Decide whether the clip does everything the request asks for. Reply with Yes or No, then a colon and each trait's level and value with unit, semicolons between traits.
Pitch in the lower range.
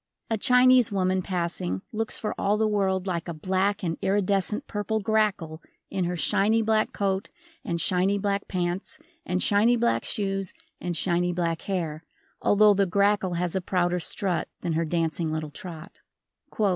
No: high, 190 Hz